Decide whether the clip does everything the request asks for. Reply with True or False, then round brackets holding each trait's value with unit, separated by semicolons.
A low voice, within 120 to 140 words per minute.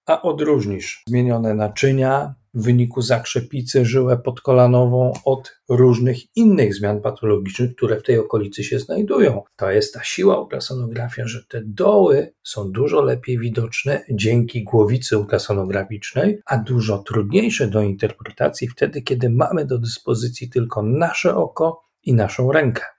True (125 Hz; 135 wpm)